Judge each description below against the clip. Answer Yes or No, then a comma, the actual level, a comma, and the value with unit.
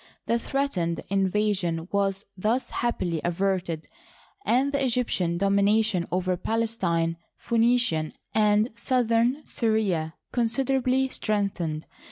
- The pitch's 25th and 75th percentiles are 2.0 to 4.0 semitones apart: No, average, 5.0 semitones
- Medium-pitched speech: No, high, 210 Hz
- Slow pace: Yes, slow, 105 wpm